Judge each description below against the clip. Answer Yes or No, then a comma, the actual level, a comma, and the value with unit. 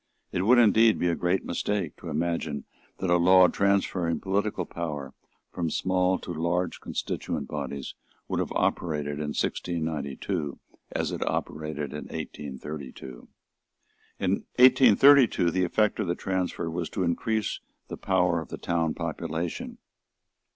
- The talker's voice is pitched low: Yes, very low, 85 Hz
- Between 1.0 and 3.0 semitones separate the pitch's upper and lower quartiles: No, average, 3.6 semitones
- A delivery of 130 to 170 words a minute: Yes, slow, 135 wpm